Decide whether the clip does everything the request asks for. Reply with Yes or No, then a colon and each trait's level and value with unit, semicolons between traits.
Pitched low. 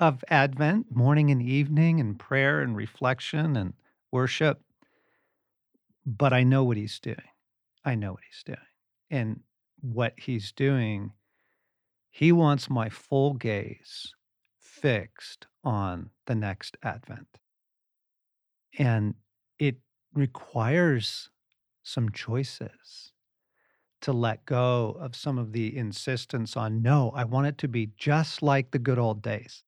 Yes: low, 125 Hz